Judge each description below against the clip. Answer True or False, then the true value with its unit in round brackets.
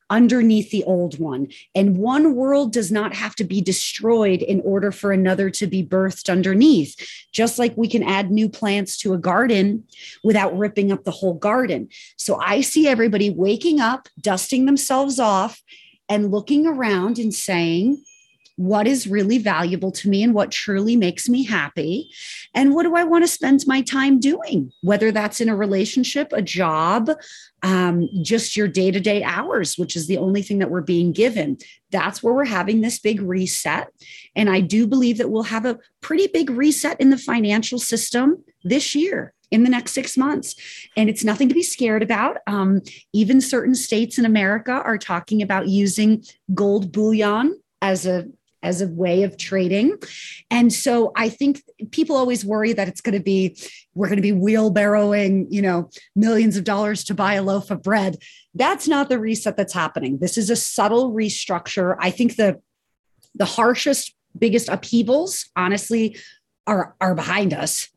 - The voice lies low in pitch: False (215 Hz)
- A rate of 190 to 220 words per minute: False (180 wpm)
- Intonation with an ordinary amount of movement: True (4.2 semitones)